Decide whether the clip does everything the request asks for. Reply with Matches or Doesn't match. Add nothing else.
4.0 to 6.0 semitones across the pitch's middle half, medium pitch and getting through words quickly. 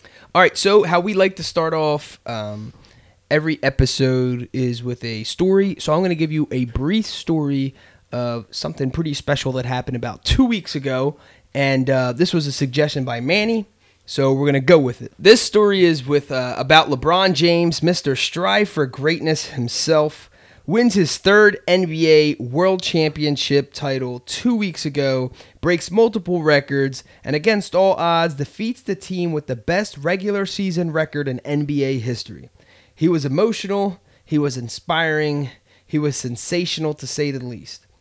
Doesn't match